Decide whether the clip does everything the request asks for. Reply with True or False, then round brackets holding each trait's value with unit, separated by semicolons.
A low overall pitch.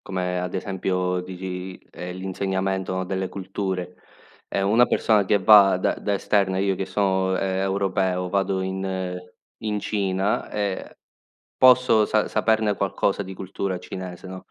True (95 Hz)